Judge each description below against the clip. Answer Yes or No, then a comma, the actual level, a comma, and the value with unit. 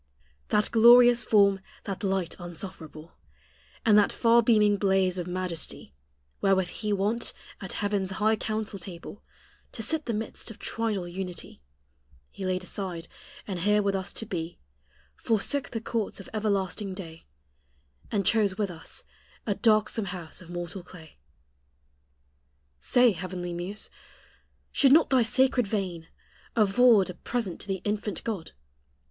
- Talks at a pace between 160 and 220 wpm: No, average, 140 wpm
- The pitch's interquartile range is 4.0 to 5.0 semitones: No, average, 3.3 semitones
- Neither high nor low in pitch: No, high, 200 Hz